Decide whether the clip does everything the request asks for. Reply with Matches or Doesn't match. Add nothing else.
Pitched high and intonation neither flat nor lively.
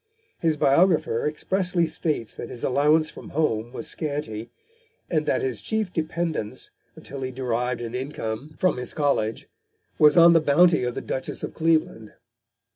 Doesn't match